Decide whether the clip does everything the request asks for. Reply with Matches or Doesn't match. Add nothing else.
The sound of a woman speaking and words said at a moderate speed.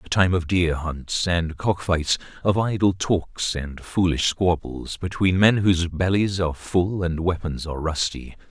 Doesn't match